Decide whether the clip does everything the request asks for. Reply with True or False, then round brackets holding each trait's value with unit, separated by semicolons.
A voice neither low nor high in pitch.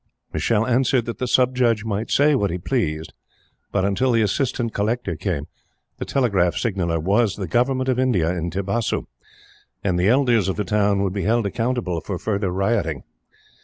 False (105 Hz)